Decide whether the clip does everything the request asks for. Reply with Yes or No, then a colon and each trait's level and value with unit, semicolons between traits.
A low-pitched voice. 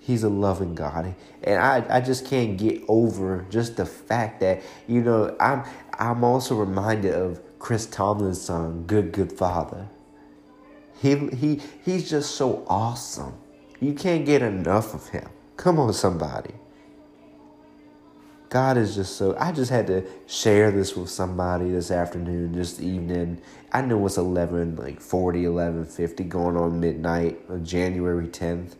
Yes: very low, 95 Hz